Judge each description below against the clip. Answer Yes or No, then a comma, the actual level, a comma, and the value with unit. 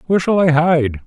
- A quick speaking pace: Yes, fast, 225 wpm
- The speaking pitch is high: No, medium, 155 Hz